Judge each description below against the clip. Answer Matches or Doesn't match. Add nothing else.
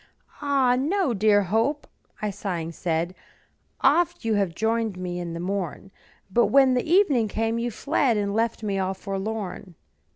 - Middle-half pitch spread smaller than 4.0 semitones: Doesn't match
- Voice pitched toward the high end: Matches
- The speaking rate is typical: Matches